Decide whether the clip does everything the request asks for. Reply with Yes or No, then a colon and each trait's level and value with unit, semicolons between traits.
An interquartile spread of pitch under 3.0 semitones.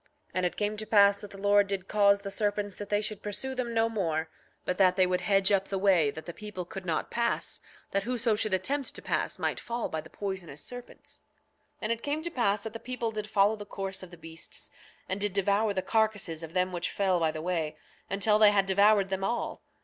Yes: narrow, 2.5 semitones